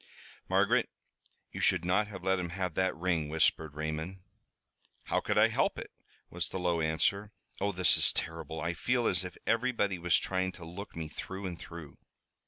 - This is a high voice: No, very low, 90 Hz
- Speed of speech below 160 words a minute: No, average, 185 wpm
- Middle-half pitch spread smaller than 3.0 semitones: Yes, narrow, 2.6 semitones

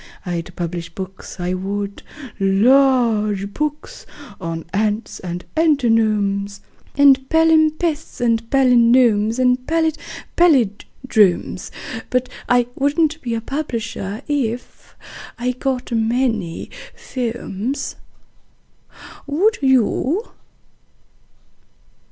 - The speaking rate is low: Yes, slow, 85 wpm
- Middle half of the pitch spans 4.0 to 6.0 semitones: Yes, average, 5.2 semitones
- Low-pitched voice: No, high, 240 Hz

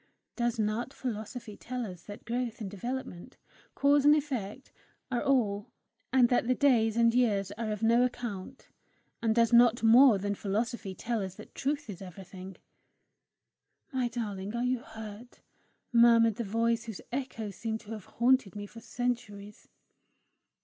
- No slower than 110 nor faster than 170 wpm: Yes, average, 155 wpm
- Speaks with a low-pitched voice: No, high, 230 Hz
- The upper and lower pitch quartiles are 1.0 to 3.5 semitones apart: Yes, average, 3.0 semitones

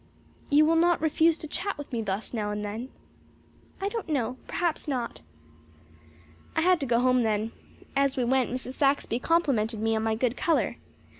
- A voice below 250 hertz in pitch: No, very high, 260 Hz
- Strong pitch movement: Yes, wide, 5.9 semitones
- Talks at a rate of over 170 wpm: Yes, average, 180 wpm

